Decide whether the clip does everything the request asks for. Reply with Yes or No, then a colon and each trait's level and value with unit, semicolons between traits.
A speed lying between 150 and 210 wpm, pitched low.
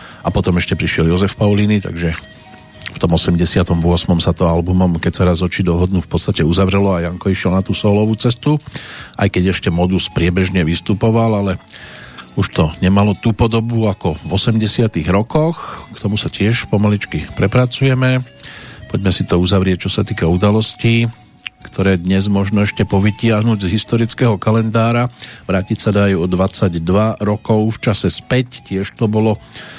Yes: average, 155 wpm; low, 100 Hz